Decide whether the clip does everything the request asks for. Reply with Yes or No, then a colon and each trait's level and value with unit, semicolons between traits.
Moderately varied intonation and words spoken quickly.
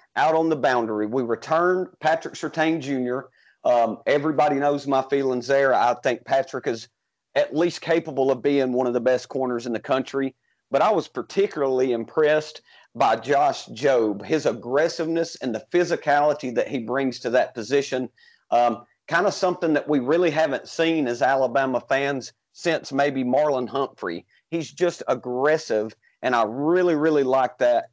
No: average, 3.8 semitones; average, 165 wpm